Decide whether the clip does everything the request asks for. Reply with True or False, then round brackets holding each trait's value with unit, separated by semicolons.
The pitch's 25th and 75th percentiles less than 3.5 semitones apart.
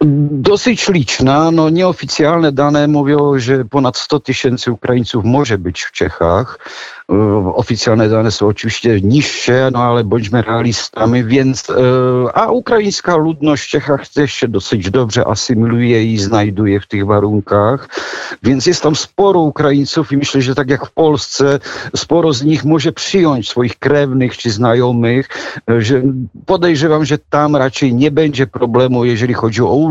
False (4.0 semitones)